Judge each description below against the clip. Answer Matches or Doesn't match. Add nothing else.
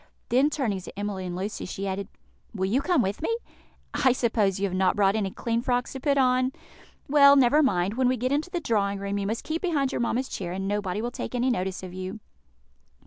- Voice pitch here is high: Matches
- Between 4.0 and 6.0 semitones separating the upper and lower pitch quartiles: Matches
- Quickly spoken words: Matches